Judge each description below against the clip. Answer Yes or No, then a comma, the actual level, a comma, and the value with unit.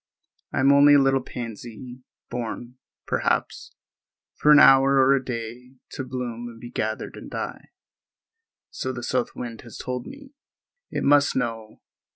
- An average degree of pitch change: No, narrow, 2.2 semitones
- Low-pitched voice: Yes, low, 125 Hz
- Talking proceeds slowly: No, average, 150 wpm